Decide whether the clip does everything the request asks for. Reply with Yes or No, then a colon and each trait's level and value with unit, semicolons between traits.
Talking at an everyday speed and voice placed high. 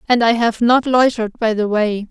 No: fast, 230 wpm; high, 230 Hz